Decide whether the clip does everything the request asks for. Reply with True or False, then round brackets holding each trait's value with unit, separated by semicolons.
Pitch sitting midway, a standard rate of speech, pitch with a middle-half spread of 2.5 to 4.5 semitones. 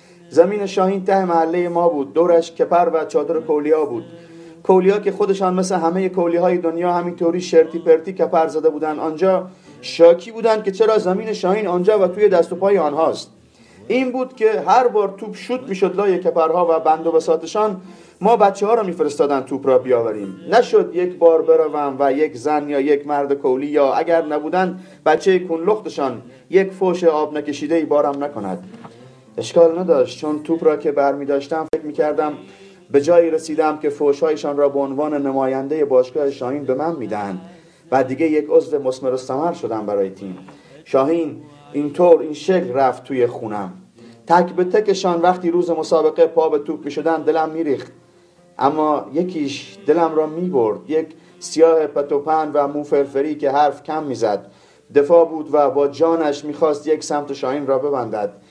False (165 Hz; 175 wpm; 3.9 semitones)